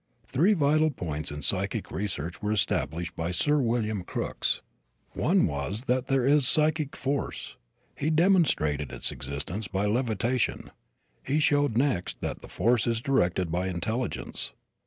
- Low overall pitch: Yes, low, 110 Hz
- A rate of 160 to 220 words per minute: No, average, 140 wpm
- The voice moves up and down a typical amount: No, wide, 8.2 semitones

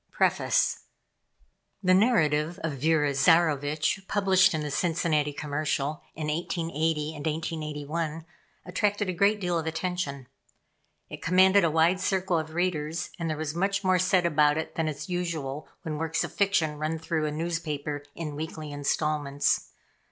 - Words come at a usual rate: Yes, average, 150 wpm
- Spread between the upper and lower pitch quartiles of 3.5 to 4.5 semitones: No, average, 2.9 semitones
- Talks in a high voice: No, medium, 160 Hz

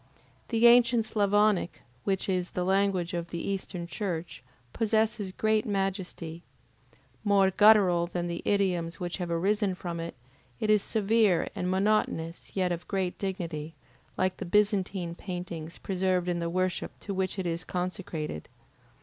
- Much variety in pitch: No, average, 2.9 semitones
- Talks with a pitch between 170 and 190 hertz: Yes, medium, 185 Hz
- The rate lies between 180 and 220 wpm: No, average, 145 wpm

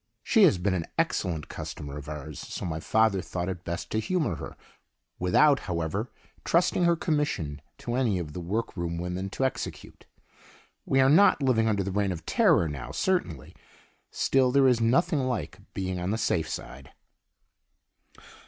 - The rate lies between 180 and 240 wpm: No, average, 165 wpm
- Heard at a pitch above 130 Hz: No, low, 100 Hz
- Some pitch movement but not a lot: No, wide, 7.5 semitones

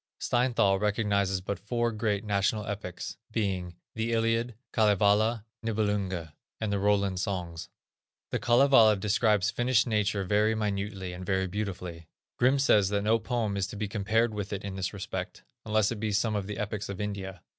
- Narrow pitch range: Yes, narrow, 2.2 semitones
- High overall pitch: No, low, 105 Hz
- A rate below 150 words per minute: No, average, 165 wpm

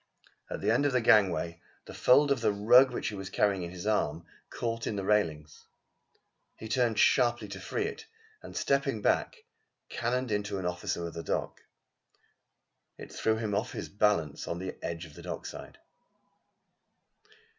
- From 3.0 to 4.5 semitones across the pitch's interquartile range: No, average, 5.0 semitones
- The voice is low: Yes, low, 105 Hz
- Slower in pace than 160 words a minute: No, average, 170 wpm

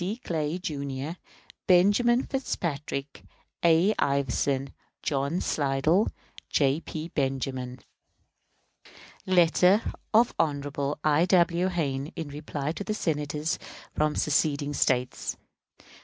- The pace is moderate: No, slow, 90 wpm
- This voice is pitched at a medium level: Yes, medium, 150 Hz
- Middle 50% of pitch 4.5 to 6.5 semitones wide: No, average, 4.0 semitones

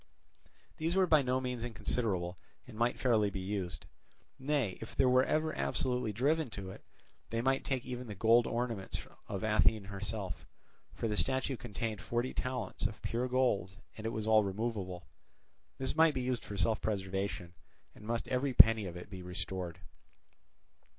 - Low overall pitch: Yes, low, 115 Hz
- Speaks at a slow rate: No, average, 170 wpm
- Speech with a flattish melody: No, average, 4.4 semitones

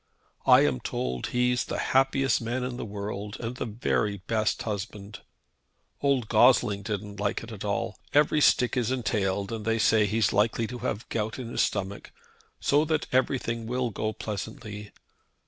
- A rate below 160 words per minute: No, average, 170 wpm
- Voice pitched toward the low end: Yes, low, 110 Hz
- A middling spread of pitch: Yes, average, 3.1 semitones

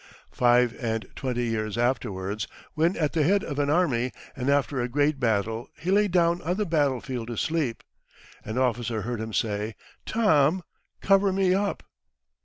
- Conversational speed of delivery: Yes, average, 165 wpm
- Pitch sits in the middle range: No, low, 130 Hz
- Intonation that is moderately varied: No, wide, 6.4 semitones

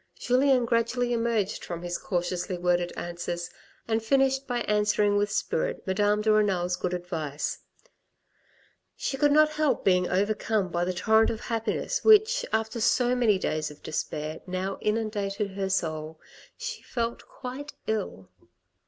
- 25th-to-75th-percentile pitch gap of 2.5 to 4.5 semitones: No, average, 5.1 semitones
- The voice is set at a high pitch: Yes, high, 210 Hz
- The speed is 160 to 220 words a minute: No, average, 145 wpm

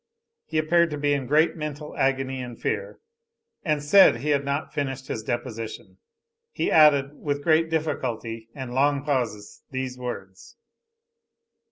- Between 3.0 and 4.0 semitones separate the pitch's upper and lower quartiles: Yes, average, 3.5 semitones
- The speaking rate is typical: Yes, average, 145 wpm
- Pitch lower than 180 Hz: Yes, medium, 140 Hz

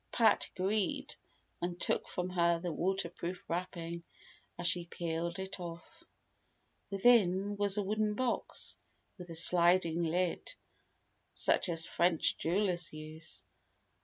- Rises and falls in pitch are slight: Yes, narrow, 2.3 semitones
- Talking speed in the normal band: No, slow, 120 wpm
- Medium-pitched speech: Yes, medium, 180 Hz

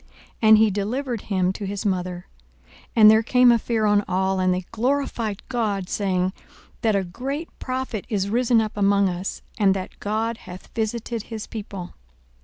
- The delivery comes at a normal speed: Yes, average, 175 wpm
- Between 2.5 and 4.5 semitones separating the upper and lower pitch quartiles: Yes, average, 3.3 semitones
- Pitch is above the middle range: Yes, high, 210 Hz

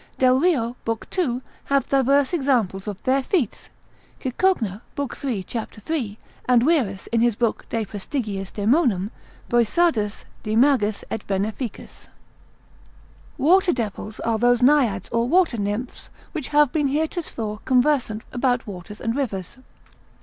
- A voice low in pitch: No, high, 240 Hz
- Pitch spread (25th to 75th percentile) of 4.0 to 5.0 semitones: Yes, average, 4.7 semitones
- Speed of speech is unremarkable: No, slow, 130 wpm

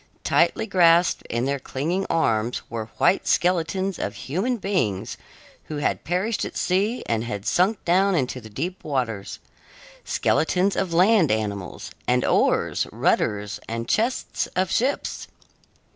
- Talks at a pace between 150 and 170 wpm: No, slow, 135 wpm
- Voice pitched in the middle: Yes, medium, 165 Hz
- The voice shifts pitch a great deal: Yes, wide, 8.5 semitones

